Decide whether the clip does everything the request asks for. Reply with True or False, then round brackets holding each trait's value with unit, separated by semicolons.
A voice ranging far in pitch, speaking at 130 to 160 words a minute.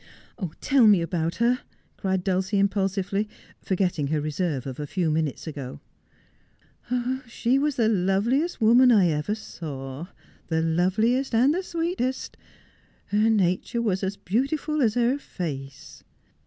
True (6.3 semitones; 140 wpm)